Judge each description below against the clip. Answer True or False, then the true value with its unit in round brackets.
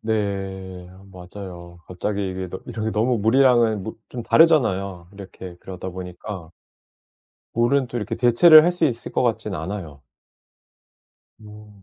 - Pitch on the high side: False (105 Hz)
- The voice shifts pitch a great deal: False (4.0 semitones)